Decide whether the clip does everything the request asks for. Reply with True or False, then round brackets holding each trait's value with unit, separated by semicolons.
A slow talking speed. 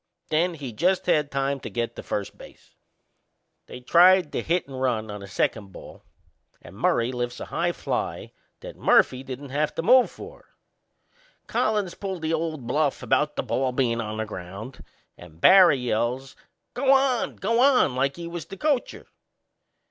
False (170 wpm)